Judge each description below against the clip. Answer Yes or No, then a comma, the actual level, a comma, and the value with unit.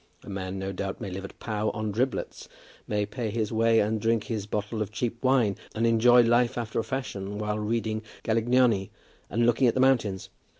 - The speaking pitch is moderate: No, low, 110 Hz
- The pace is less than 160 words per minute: No, average, 200 wpm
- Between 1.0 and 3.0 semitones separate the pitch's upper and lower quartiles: Yes, narrow, 2.4 semitones